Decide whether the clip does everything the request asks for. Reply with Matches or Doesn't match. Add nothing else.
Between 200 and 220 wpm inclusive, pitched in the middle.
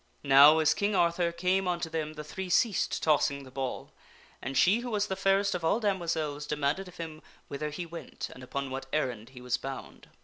Matches